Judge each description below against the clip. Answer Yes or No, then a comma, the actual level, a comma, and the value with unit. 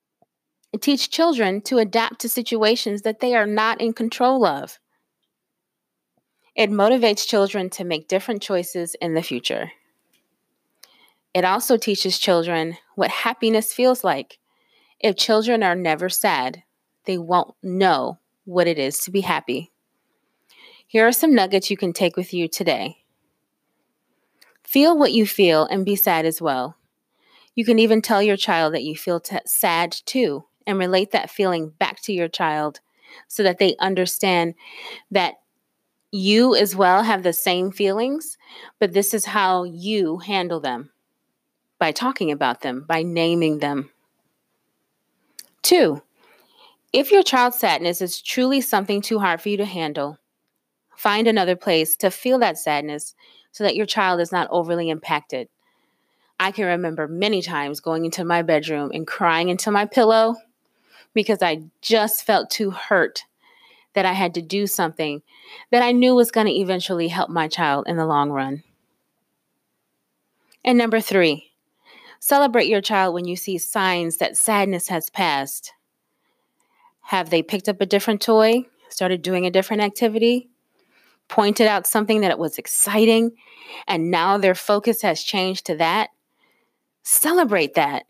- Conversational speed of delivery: Yes, average, 150 wpm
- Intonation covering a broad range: No, average, 4.6 semitones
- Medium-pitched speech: No, high, 195 Hz